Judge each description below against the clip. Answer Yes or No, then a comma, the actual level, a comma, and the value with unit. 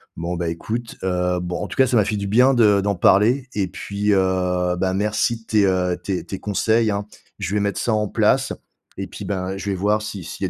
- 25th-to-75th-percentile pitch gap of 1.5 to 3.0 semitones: Yes, narrow, 2.4 semitones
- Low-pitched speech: Yes, low, 100 Hz